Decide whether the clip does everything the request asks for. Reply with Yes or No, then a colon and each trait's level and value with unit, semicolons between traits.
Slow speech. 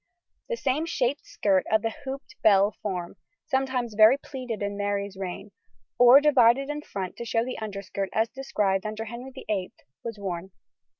No: average, 165 wpm